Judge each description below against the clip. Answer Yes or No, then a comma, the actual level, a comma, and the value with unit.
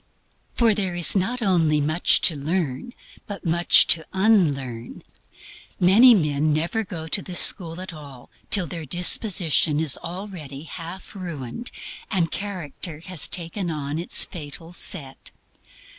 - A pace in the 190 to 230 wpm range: No, slow, 135 wpm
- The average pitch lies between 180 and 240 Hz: No, medium, 170 Hz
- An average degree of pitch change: Yes, average, 3.9 semitones